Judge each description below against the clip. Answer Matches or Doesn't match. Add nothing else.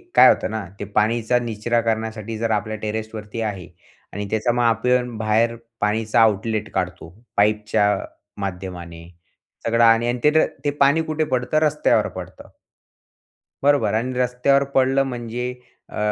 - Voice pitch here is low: Matches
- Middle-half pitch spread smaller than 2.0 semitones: Doesn't match